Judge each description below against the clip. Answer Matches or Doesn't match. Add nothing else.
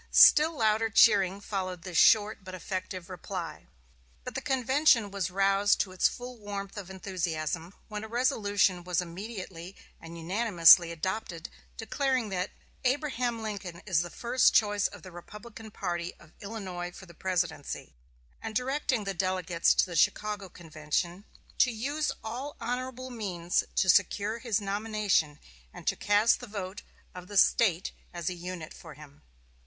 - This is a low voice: Doesn't match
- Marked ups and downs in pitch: Doesn't match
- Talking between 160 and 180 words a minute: Doesn't match